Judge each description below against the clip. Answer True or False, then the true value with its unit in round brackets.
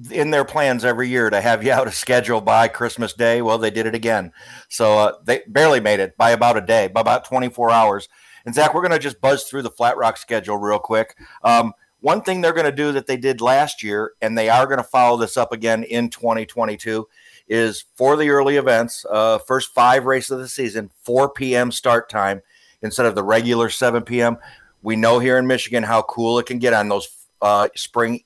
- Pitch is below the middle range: True (120 Hz)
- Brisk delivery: True (225 wpm)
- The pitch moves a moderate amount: False (2.3 semitones)